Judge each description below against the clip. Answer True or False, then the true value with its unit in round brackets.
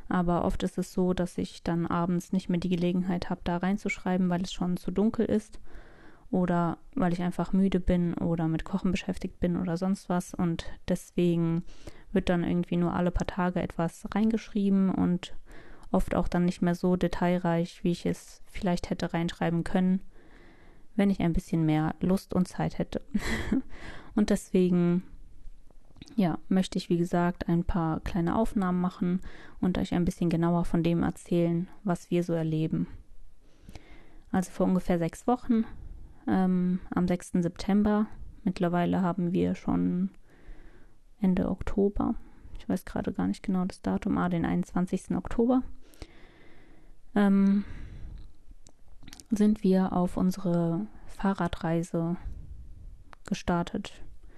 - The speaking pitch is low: False (180 Hz)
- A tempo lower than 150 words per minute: True (140 wpm)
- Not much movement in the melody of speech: True (2.1 semitones)